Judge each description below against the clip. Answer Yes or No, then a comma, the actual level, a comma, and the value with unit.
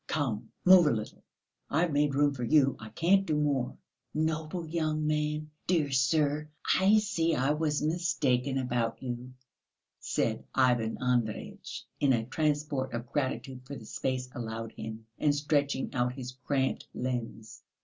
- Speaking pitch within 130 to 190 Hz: Yes, medium, 140 Hz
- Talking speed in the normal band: Yes, average, 150 wpm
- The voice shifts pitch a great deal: No, average, 3.6 semitones